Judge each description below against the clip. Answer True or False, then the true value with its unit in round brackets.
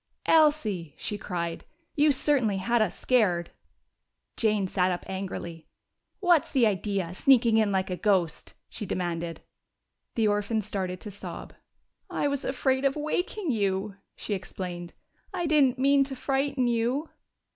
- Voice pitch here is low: False (215 Hz)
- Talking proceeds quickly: False (140 wpm)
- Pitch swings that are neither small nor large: False (6.4 semitones)